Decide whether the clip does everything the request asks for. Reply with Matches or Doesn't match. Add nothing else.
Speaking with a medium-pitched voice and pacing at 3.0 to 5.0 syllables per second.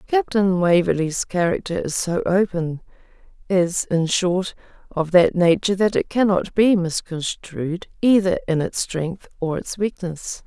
Matches